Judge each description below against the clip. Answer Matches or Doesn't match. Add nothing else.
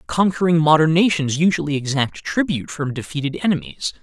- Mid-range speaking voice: Matches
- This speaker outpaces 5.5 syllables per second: Matches